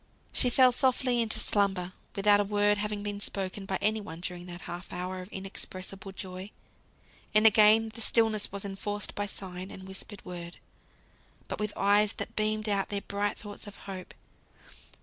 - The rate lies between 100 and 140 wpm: No, average, 170 wpm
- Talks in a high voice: Yes, high, 200 Hz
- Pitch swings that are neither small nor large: No, narrow, 2.0 semitones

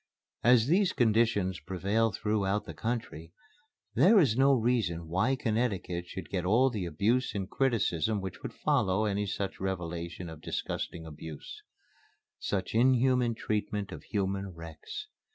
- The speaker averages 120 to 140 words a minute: Yes, slow, 135 wpm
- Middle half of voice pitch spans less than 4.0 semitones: No, average, 4.6 semitones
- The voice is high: No, low, 105 Hz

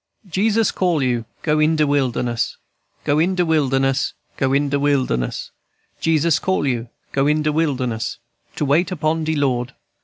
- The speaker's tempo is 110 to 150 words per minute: No, average, 160 wpm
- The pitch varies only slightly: No, average, 3.4 semitones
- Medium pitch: Yes, medium, 145 Hz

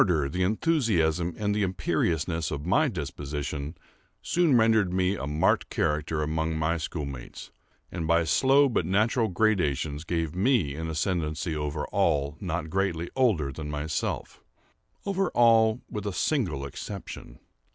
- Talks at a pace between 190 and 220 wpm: No, average, 150 wpm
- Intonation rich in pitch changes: Yes, wide, 5.7 semitones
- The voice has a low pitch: Yes, very low, 85 Hz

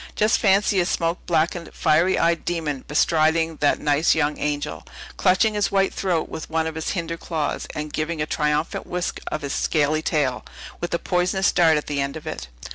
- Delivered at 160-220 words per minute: Yes, average, 195 wpm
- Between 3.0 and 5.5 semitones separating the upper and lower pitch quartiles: No, narrow, 2.6 semitones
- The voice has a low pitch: No, medium, 160 Hz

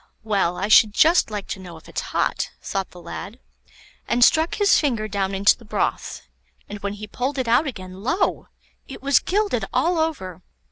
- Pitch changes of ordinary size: No, wide, 6.4 semitones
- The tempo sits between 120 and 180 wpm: No, average, 190 wpm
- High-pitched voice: Yes, high, 215 Hz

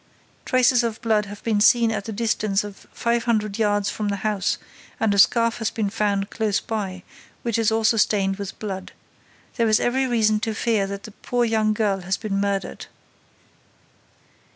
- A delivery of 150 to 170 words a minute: No, average, 180 wpm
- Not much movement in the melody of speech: Yes, narrow, 2.2 semitones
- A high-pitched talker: Yes, high, 215 Hz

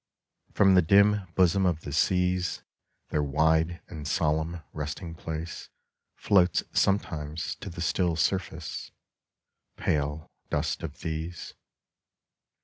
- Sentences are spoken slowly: Yes, slow, 110 wpm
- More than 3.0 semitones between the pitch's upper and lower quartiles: No, narrow, 2.6 semitones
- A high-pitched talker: No, very low, 85 Hz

